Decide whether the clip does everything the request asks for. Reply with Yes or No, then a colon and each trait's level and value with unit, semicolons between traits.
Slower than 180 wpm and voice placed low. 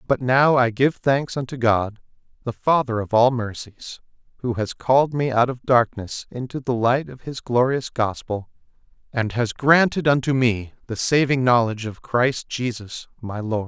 Yes: average, 170 wpm; low, 125 Hz